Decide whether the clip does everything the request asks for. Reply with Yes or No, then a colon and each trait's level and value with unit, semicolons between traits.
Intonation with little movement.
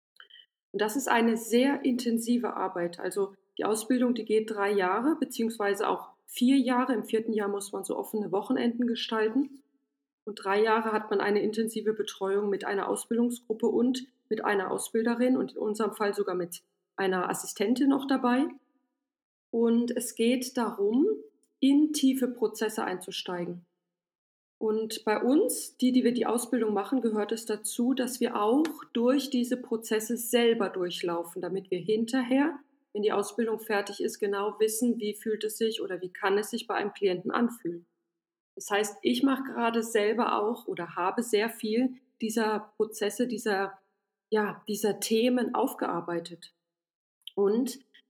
No: average, 3.5 semitones